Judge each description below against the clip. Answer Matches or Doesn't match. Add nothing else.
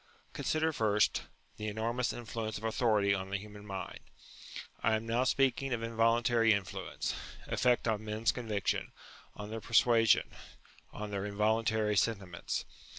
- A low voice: Matches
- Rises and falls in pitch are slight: Matches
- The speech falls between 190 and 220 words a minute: Doesn't match